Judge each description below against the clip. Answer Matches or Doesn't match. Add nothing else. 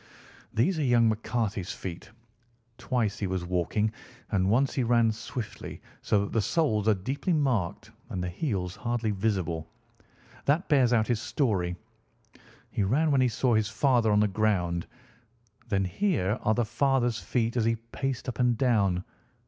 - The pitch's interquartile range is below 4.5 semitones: Matches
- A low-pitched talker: Matches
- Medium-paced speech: Matches